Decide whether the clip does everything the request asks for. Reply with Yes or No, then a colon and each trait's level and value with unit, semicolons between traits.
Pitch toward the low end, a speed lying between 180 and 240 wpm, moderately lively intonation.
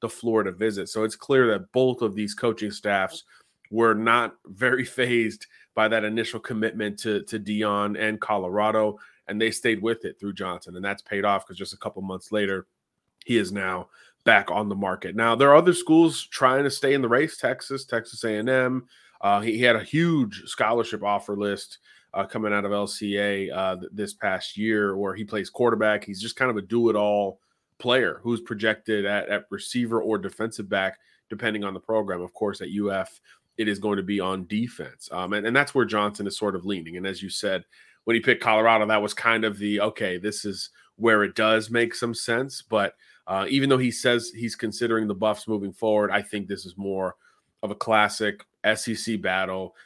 No: low, 110 Hz; fast, 205 wpm; narrow, 2.2 semitones